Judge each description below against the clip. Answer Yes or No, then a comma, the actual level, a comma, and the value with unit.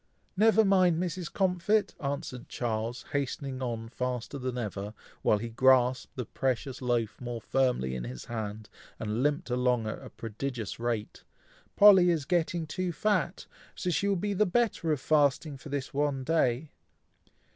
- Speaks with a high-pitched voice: No, low, 135 Hz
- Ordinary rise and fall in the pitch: No, wide, 6.2 semitones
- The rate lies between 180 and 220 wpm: No, average, 155 wpm